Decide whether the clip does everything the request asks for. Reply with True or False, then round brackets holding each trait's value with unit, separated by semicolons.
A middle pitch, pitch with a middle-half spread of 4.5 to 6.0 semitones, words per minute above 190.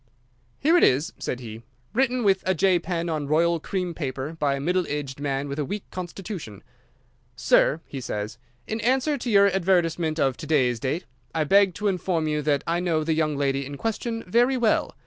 True (165 Hz; 5.3 semitones; 200 wpm)